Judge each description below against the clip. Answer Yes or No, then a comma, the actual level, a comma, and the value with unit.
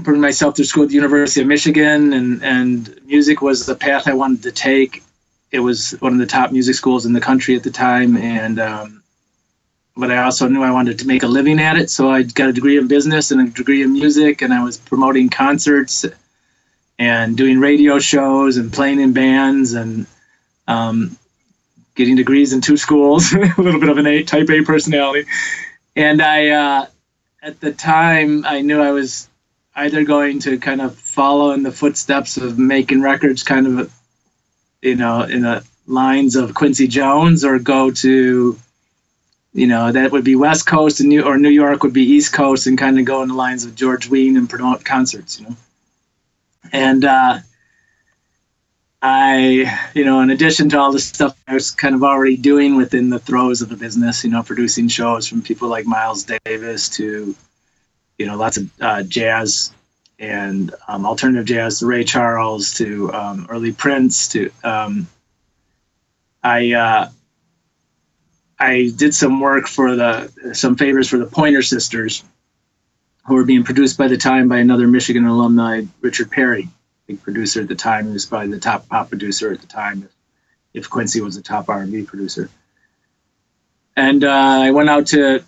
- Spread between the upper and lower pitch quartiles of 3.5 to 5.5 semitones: No, average, 2.9 semitones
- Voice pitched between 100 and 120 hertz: No, low, 130 Hz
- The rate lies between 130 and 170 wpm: No, average, 185 wpm